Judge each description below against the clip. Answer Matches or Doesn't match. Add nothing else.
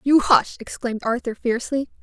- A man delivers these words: Doesn't match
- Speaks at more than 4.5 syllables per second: Matches